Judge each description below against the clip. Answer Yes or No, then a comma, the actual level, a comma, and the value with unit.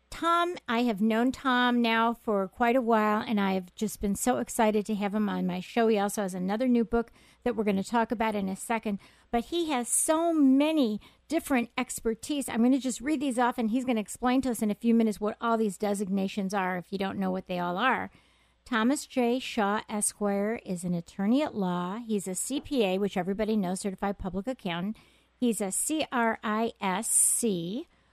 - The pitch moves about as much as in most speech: Yes, average, 3.6 semitones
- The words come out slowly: No, fast, 205 wpm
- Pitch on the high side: Yes, high, 220 Hz